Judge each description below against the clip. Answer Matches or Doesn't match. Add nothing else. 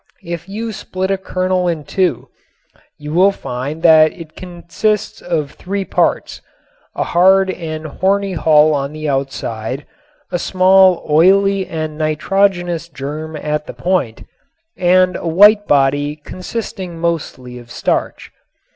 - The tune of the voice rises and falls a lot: Doesn't match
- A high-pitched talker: Doesn't match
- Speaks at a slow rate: Matches